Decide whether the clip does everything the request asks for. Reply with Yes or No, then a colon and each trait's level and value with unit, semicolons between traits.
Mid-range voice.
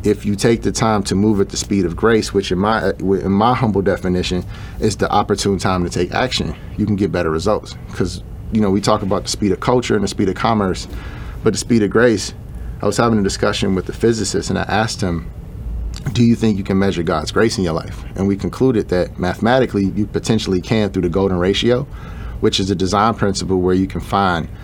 No: low, 100 Hz